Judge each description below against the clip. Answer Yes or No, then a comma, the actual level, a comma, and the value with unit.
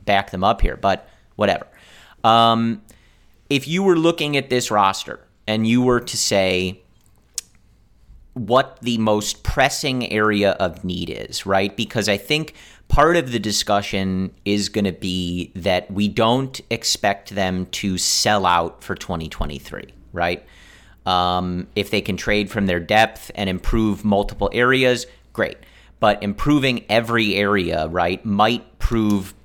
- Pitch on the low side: Yes, low, 100 Hz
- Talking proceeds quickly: No, average, 145 wpm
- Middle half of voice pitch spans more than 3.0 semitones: Yes, average, 3.5 semitones